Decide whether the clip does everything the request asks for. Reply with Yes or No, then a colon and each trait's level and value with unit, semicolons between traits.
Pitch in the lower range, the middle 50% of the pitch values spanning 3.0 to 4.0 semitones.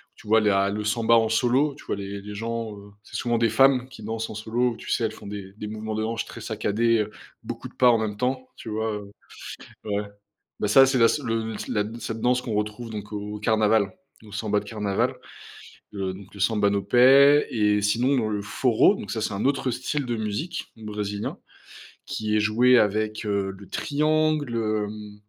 No: low, 110 Hz; narrow, 2.4 semitones